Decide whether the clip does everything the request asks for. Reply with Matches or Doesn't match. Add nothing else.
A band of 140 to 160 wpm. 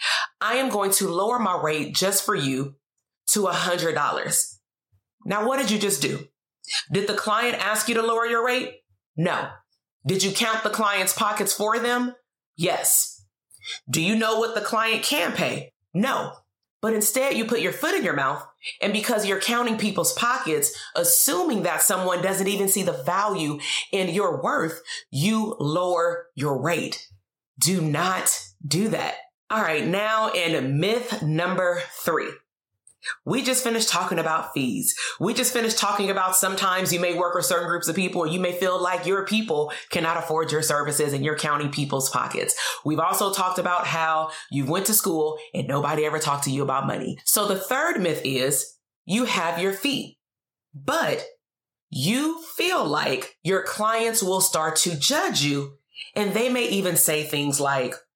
Doesn't match